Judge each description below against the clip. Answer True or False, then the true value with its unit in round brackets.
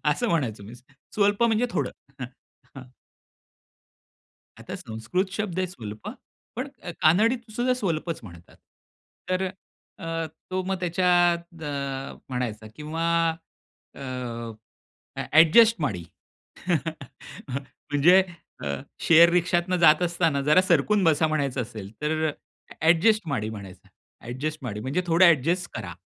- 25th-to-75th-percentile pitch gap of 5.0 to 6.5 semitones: True (5.3 semitones)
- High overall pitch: False (160 Hz)